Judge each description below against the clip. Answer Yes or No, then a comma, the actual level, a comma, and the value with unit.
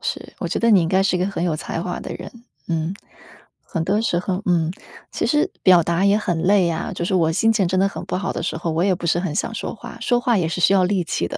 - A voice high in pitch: No, medium, 180 Hz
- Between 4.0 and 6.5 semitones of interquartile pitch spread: No, average, 2.7 semitones